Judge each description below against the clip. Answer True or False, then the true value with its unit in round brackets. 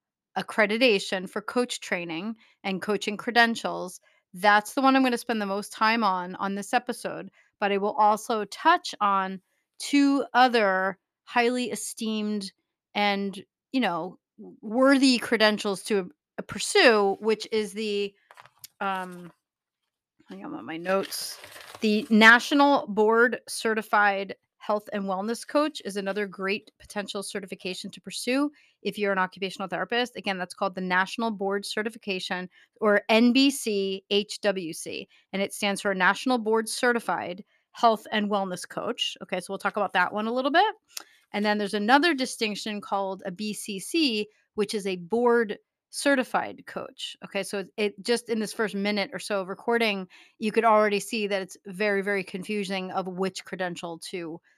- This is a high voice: True (205 Hz)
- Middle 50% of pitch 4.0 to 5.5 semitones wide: False (2.8 semitones)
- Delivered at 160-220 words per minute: False (150 wpm)